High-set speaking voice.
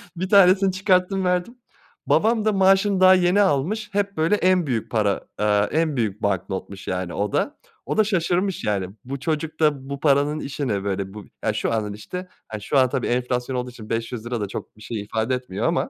No: medium, 140 Hz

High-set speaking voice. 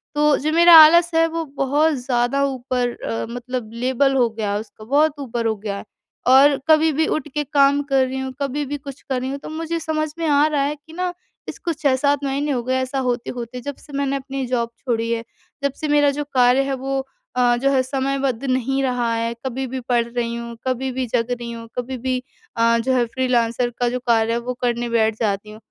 Yes: very high, 260 Hz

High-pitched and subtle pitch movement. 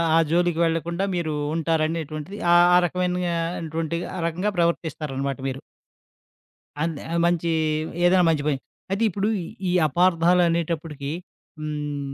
No: medium, 165 Hz; narrow, 2.3 semitones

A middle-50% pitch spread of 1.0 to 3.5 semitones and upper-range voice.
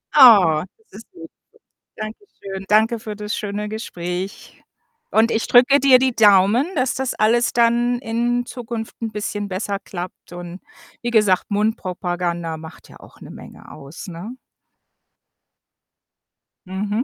No: average, 4.0 semitones; high, 215 Hz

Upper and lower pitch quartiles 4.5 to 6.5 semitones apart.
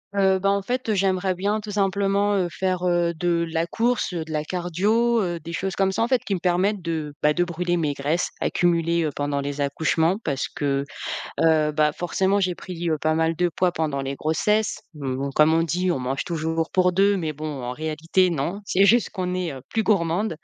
No: average, 3.5 semitones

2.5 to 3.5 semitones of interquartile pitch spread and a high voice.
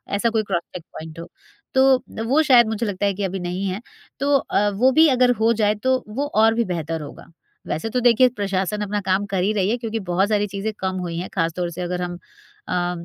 No: average, 4.2 semitones; high, 205 Hz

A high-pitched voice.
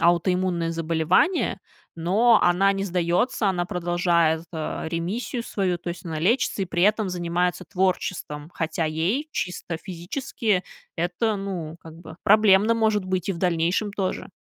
No: medium, 180 Hz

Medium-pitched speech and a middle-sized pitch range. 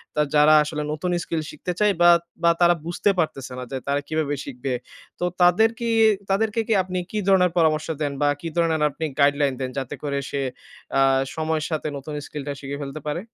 Yes: medium, 155 Hz; average, 3.4 semitones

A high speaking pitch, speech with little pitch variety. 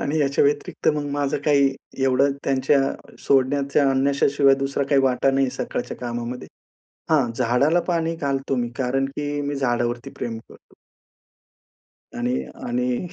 No: low, 135 Hz; narrow, 2.2 semitones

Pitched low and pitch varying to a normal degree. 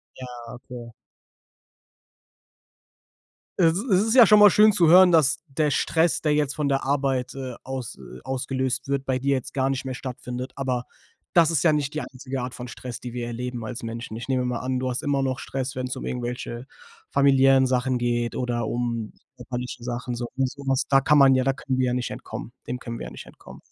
No: low, 130 Hz; narrow, 2.0 semitones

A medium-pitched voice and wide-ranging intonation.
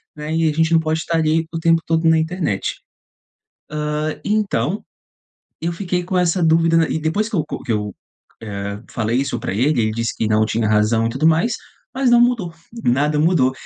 Yes: medium, 160 Hz; wide, 6.3 semitones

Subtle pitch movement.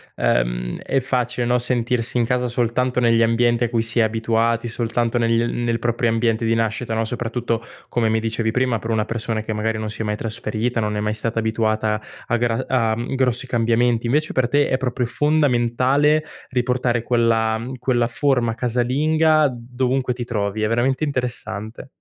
Yes: narrow, 1.8 semitones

